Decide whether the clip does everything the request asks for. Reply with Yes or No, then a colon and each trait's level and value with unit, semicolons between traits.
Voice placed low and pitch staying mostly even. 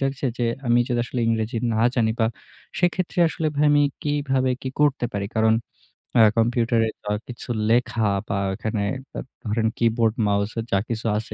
No: low, 115 Hz; average, 3.0 semitones